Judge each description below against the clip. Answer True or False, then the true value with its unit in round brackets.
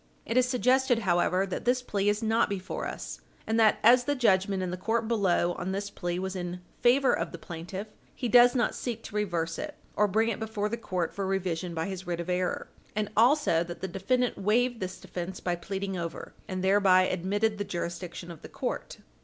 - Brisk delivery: True (210 wpm)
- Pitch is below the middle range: False (195 Hz)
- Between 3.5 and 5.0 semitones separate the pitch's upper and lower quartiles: True (4.0 semitones)